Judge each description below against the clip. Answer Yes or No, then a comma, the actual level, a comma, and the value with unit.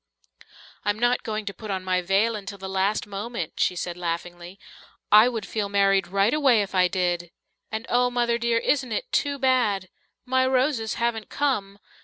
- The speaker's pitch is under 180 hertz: No, high, 210 Hz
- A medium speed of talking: Yes, average, 180 wpm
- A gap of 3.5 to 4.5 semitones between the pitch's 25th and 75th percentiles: Yes, average, 3.9 semitones